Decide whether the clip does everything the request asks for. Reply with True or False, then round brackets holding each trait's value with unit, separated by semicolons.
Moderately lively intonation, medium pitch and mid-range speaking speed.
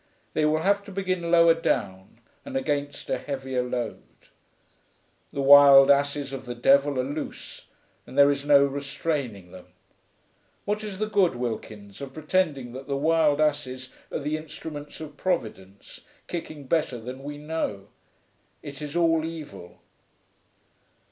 True (3.5 semitones; 145 Hz; 145 wpm)